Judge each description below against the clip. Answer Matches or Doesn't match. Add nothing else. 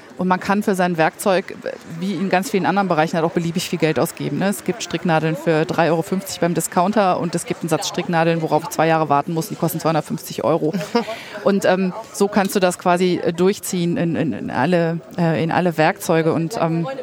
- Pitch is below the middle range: Doesn't match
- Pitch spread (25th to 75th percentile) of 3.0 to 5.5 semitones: Doesn't match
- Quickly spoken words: Matches